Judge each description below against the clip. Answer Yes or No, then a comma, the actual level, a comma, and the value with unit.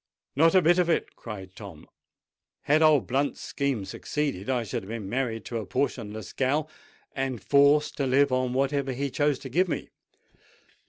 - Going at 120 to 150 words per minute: No, average, 175 wpm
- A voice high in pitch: No, low, 135 Hz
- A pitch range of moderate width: Yes, average, 4.0 semitones